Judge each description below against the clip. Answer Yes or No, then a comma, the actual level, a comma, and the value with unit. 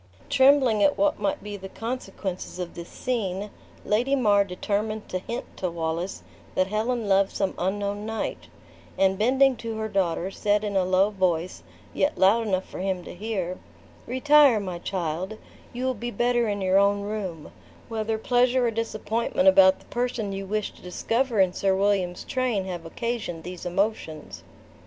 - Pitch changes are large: No, average, 3.8 semitones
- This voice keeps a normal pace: Yes, average, 170 wpm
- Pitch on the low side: No, high, 205 Hz